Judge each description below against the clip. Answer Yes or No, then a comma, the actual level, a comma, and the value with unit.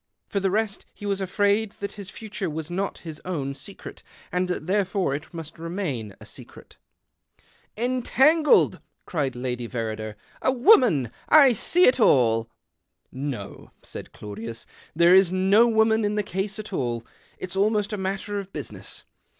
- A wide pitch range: Yes, wide, 6.8 semitones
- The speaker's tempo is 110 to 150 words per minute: No, average, 175 wpm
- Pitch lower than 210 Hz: Yes, high, 190 Hz